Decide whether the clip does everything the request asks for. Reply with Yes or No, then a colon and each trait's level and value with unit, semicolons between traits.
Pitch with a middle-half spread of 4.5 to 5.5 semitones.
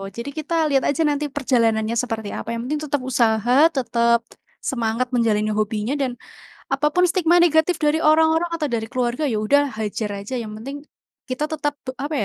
Yes: average, 4.8 semitones